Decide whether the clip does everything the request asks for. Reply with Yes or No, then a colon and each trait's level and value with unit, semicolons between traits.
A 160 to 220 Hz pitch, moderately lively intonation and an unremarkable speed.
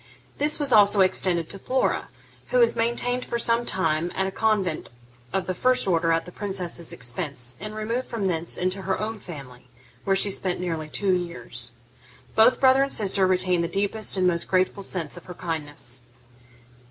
Yes: medium, 185 Hz; average, 4.2 semitones; average, 180 wpm